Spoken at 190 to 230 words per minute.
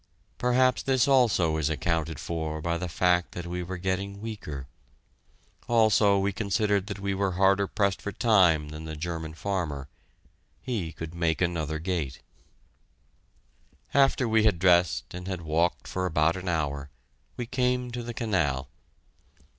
No: average, 150 wpm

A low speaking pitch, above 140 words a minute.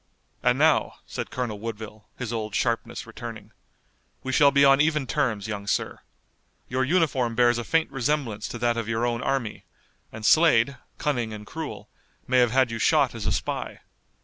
Yes: low, 120 Hz; average, 175 wpm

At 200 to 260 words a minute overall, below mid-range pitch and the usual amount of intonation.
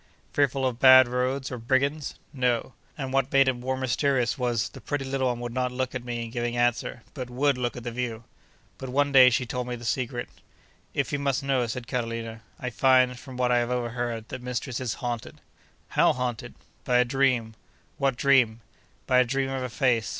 No: fast, 205 wpm; low, 125 Hz; narrow, 1.8 semitones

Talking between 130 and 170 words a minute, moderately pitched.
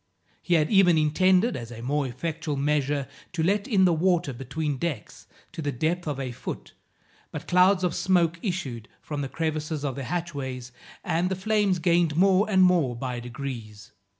No: average, 180 wpm; medium, 160 Hz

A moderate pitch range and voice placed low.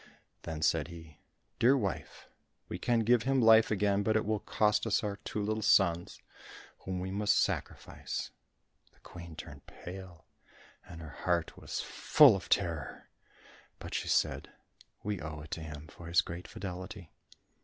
Yes: average, 4.2 semitones; very low, 95 Hz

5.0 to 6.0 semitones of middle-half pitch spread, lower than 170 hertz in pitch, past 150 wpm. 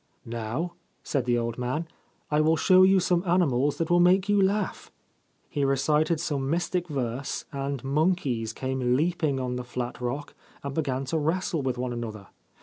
Yes: wide, 5.4 semitones; medium, 140 Hz; average, 180 wpm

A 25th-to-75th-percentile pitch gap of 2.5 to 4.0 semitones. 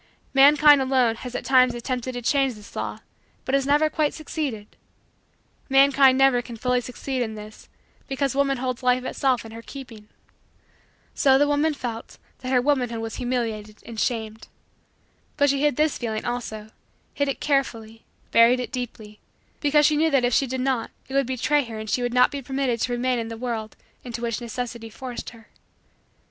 Yes: average, 2.9 semitones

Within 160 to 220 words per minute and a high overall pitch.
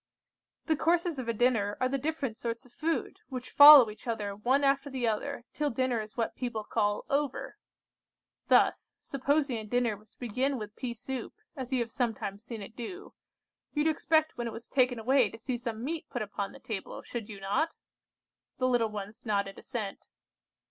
Yes: average, 195 wpm; high, 245 Hz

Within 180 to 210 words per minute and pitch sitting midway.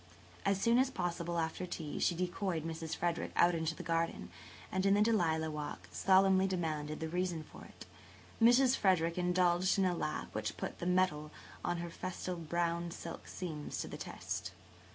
Yes: average, 190 wpm; medium, 175 Hz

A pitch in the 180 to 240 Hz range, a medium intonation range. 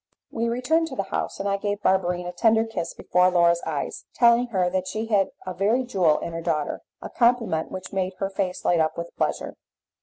Yes: high, 190 Hz; average, 4.3 semitones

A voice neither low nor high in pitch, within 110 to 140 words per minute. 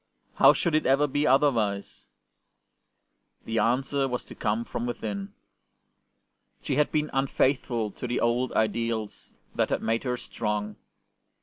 No: low, 120 Hz; slow, 135 wpm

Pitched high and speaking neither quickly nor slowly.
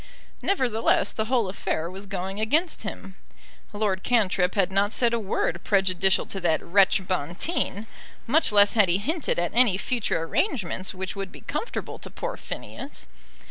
Yes: high, 200 Hz; average, 160 wpm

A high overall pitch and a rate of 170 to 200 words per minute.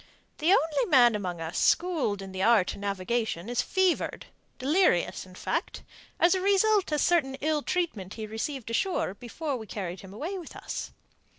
Yes: high, 245 Hz; average, 175 wpm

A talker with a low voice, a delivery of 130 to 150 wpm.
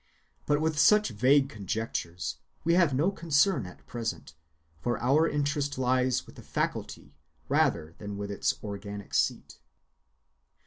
Yes: low, 130 Hz; slow, 135 wpm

